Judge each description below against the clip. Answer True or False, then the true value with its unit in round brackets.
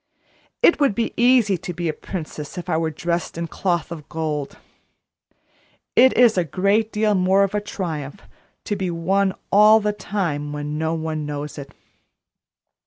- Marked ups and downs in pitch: False (4.6 semitones)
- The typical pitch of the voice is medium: True (180 Hz)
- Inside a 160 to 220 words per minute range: True (170 wpm)